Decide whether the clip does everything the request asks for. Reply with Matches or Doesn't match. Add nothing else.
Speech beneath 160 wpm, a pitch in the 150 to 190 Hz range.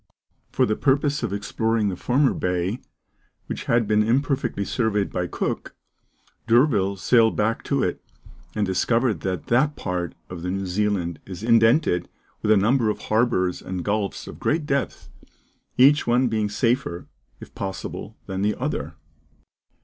Doesn't match